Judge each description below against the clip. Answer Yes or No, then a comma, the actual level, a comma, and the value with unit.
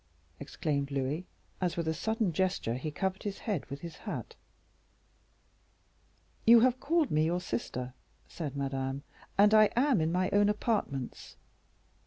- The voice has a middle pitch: Yes, medium, 175 Hz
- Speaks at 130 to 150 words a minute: Yes, average, 145 wpm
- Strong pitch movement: Yes, wide, 6.8 semitones